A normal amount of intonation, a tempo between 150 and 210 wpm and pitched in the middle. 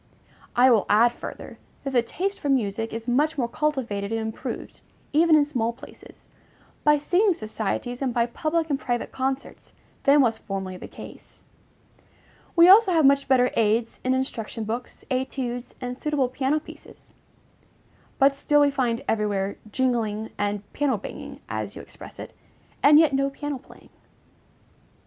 No: average, 4.2 semitones; average, 155 wpm; very high, 255 Hz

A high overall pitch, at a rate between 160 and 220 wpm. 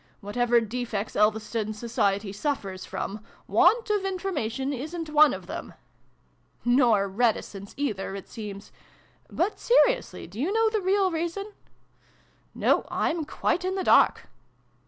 No: high, 245 Hz; average, 150 wpm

